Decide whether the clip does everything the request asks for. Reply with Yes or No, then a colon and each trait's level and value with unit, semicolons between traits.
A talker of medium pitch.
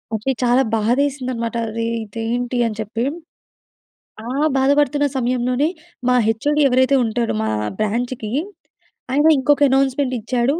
No: very high, 250 Hz